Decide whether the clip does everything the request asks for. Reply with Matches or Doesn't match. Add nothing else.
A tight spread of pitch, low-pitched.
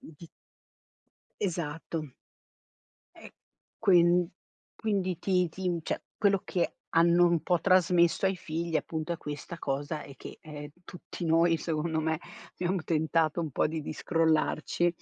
Doesn't match